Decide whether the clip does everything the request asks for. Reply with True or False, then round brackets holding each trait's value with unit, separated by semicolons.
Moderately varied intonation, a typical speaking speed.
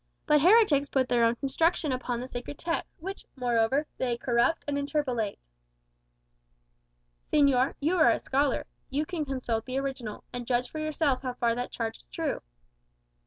True (3.6 semitones; 165 wpm)